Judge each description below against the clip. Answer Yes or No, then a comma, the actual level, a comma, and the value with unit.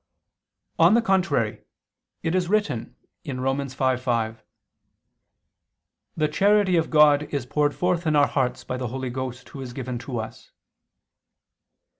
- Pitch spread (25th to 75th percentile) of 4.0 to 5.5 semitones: Yes, average, 4.6 semitones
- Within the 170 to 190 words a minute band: No, slow, 135 wpm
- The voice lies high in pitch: No, medium, 140 Hz